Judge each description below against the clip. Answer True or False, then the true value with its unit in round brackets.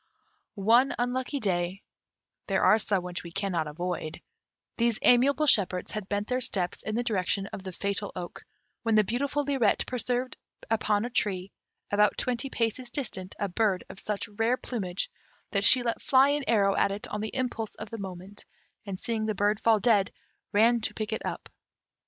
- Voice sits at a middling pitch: False (215 Hz)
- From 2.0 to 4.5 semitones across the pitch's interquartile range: True (3.6 semitones)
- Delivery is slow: False (180 wpm)